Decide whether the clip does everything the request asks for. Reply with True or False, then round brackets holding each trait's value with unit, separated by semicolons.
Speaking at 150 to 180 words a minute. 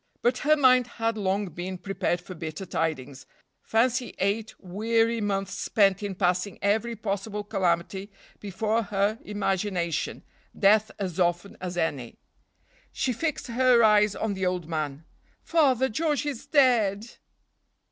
False (135 wpm)